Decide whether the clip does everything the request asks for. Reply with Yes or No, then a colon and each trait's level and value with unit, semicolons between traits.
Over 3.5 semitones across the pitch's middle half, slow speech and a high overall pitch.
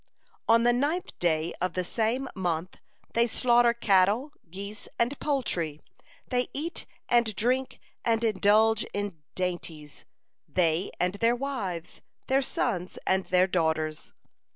Yes: average, 5.2 semitones; slow, 130 wpm; high, 205 Hz